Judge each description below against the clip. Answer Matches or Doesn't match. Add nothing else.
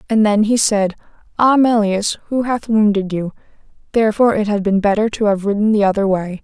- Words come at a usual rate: Matches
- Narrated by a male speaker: Doesn't match